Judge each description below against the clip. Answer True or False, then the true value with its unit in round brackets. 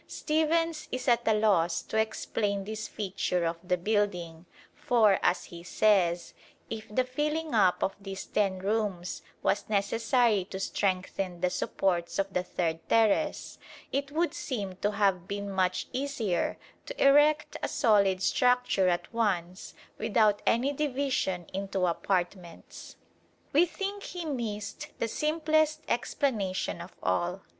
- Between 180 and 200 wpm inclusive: False (135 wpm)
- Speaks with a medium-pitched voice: False (205 Hz)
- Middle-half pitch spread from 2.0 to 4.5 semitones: False (5.6 semitones)